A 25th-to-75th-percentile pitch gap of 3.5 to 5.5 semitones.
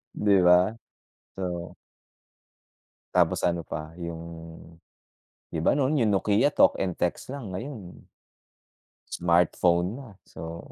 Yes: average, 4.2 semitones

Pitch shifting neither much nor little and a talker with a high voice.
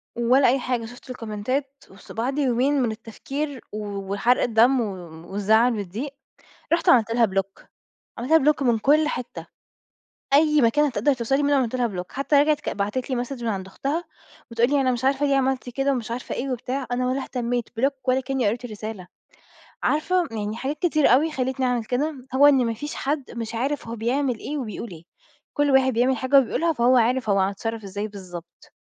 Yes: average, 3.4 semitones; very high, 250 Hz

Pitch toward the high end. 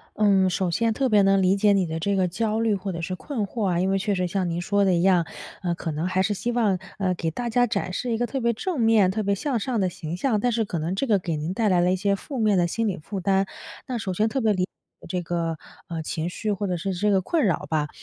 Yes: high, 195 Hz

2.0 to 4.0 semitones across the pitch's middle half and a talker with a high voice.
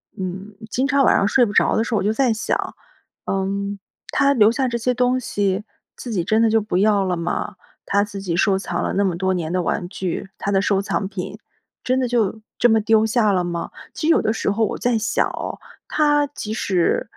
Yes: average, 3.6 semitones; high, 210 Hz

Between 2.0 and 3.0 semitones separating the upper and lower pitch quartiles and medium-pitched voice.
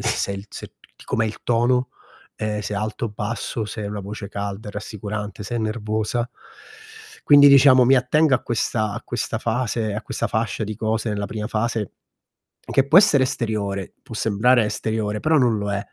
No: average, 2.7 semitones; low, 110 Hz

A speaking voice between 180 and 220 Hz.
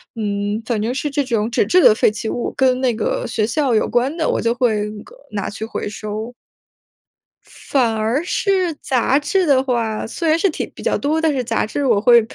No: high, 245 Hz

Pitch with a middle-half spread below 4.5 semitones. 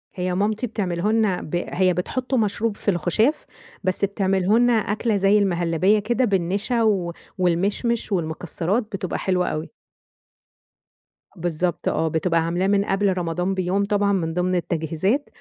Yes: average, 3.0 semitones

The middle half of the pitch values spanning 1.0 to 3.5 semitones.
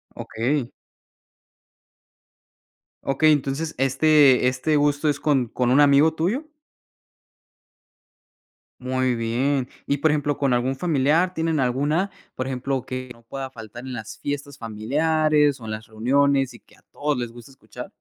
Yes: average, 3.0 semitones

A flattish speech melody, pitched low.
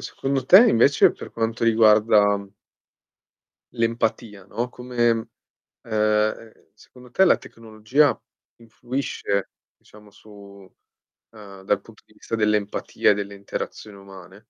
Yes: narrow, 2.3 semitones; low, 110 Hz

